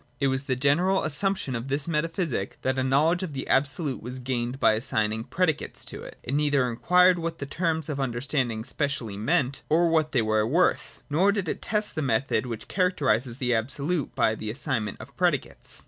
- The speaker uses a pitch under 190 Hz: Yes, medium, 140 Hz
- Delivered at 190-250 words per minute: Yes, average, 195 wpm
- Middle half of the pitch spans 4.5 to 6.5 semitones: Yes, average, 5.0 semitones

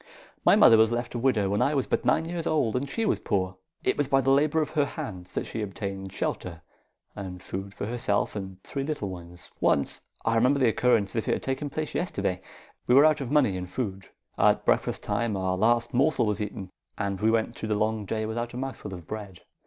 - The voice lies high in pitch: No, low, 110 Hz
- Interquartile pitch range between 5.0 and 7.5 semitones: Yes, wide, 5.6 semitones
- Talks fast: Yes, fast, 230 wpm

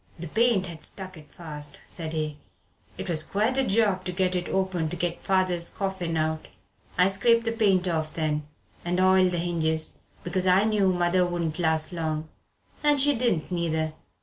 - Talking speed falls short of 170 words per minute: No, average, 180 wpm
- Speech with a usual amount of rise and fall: Yes, average, 3.2 semitones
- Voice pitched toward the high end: No, medium, 175 Hz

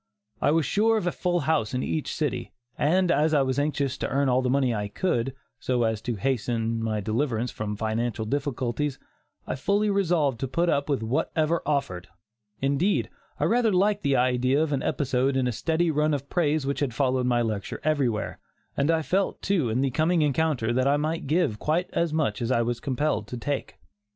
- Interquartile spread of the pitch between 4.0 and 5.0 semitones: Yes, average, 4.6 semitones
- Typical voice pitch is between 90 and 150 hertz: Yes, medium, 140 Hz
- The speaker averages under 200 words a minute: No, fast, 205 wpm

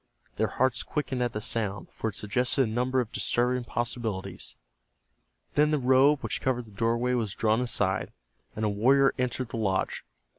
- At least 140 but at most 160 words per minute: No, average, 175 wpm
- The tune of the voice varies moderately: Yes, average, 3.0 semitones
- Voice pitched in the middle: No, low, 120 Hz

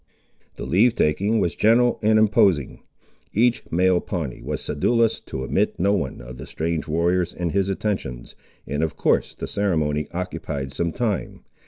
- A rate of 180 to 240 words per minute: No, average, 160 wpm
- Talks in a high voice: No, very low, 90 Hz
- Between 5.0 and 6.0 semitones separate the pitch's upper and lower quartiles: Yes, average, 5.3 semitones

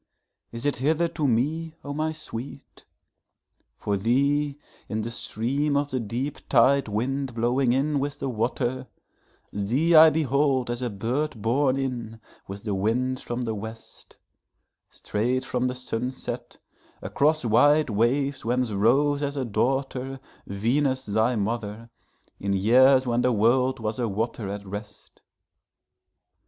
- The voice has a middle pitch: No, low, 125 Hz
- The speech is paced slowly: Yes, slow, 130 wpm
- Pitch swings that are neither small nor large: Yes, average, 3.7 semitones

